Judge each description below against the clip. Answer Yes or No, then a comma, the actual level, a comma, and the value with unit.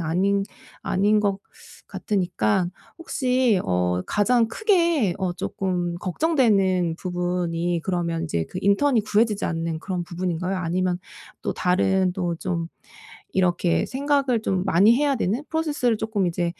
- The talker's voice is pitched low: No, medium, 185 Hz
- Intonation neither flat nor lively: Yes, average, 4.3 semitones